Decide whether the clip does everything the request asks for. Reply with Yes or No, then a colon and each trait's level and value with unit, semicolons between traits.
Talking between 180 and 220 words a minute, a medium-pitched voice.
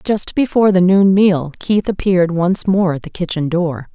Yes: average, 200 wpm; medium, 180 Hz